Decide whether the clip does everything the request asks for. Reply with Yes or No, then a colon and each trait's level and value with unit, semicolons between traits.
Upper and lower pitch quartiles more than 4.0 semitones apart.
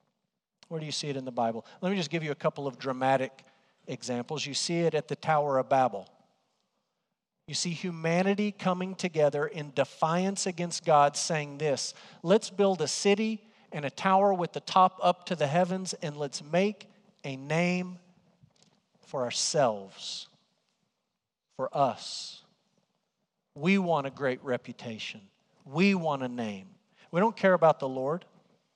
Yes: average, 5.2 semitones